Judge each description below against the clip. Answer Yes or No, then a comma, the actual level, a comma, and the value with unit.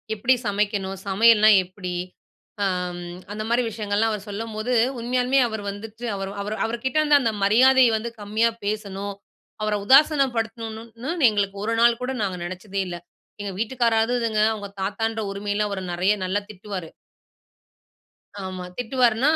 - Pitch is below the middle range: No, high, 215 Hz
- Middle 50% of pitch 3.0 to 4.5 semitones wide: No, narrow, 2.6 semitones